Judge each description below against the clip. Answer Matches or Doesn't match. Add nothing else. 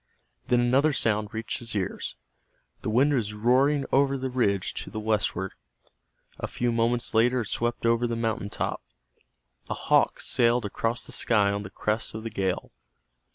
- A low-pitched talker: Matches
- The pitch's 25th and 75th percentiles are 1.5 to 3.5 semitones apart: Matches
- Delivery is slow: Doesn't match